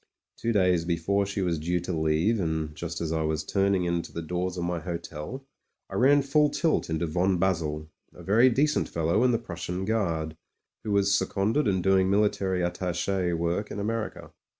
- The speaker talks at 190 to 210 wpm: Yes, average, 195 wpm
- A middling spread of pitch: Yes, average, 3.5 semitones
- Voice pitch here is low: Yes, very low, 90 Hz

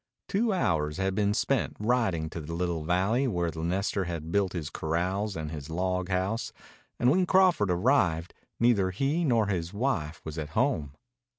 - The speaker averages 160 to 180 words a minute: Yes, average, 175 wpm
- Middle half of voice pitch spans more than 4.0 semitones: Yes, wide, 5.6 semitones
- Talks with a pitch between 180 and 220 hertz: No, very low, 95 Hz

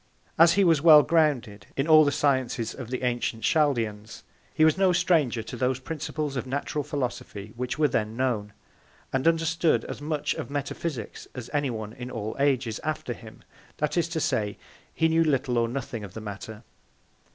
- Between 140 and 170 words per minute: No, average, 185 wpm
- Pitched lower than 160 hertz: Yes, low, 135 Hz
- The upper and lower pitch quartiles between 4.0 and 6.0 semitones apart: Yes, average, 5.1 semitones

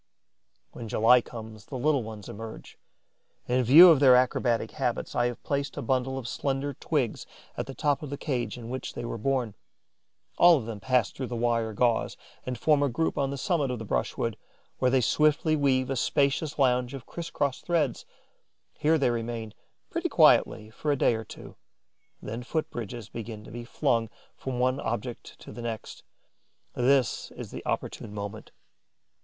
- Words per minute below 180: No, average, 185 wpm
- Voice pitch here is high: No, low, 125 Hz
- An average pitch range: Yes, average, 3.3 semitones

